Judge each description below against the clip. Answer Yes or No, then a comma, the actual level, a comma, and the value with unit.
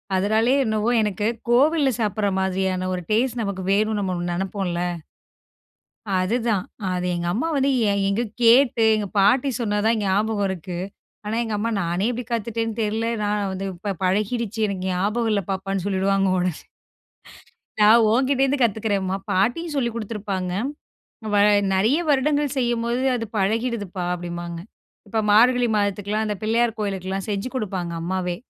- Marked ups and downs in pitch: No, average, 3.5 semitones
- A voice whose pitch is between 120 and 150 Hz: No, high, 210 Hz